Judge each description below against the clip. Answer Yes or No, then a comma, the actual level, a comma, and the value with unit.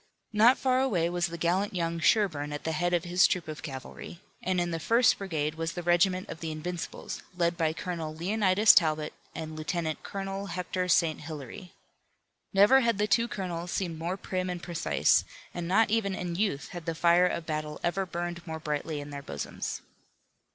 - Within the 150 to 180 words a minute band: No, average, 190 wpm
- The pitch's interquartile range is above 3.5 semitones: No, average, 2.9 semitones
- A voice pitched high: No, medium, 175 Hz